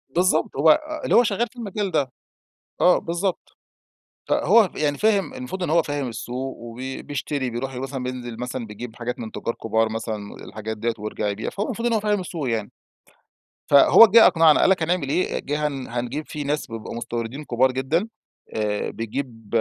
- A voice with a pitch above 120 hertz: Yes, low, 135 Hz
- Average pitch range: No, wide, 7.2 semitones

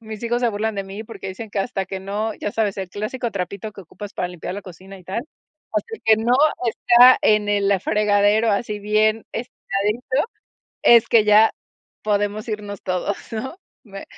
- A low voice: No, high, 210 Hz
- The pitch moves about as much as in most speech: No, narrow, 2.0 semitones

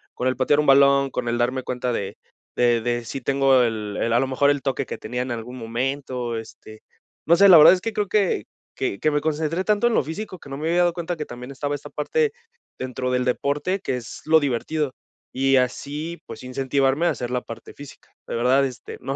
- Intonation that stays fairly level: No, average, 3.8 semitones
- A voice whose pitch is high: No, low, 135 Hz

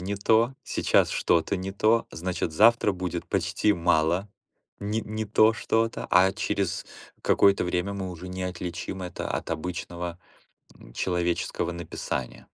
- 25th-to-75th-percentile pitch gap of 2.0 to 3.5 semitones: Yes, average, 2.8 semitones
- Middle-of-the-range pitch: No, very low, 90 Hz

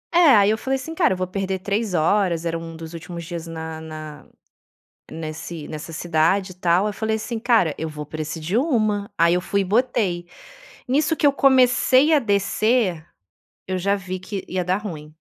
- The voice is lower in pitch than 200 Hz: Yes, medium, 185 Hz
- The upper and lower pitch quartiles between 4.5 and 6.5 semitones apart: Yes, average, 4.9 semitones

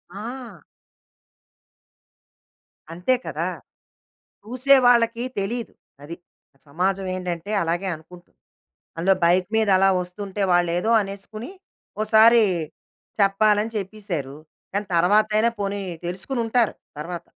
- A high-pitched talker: Yes, high, 200 Hz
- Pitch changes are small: No, average, 3.9 semitones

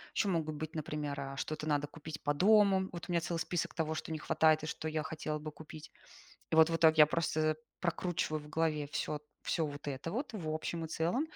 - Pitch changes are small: Yes, narrow, 1.7 semitones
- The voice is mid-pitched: Yes, medium, 155 Hz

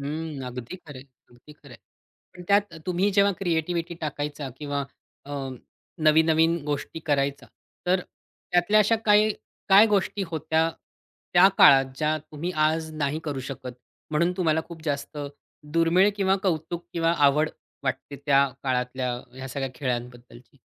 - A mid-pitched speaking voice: Yes, medium, 155 Hz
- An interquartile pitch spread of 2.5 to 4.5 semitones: Yes, average, 3.8 semitones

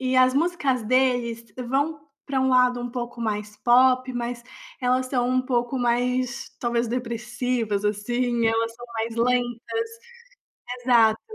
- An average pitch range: No, narrow, 1.6 semitones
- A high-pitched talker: Yes, high, 245 Hz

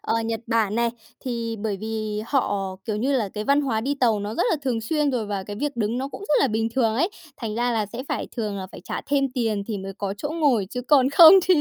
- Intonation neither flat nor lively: Yes, average, 4.2 semitones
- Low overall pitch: No, high, 230 Hz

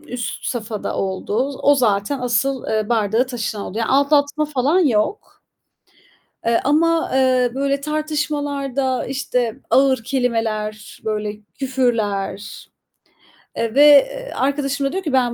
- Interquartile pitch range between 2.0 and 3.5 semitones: No, average, 4.2 semitones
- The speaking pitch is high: Yes, very high, 260 Hz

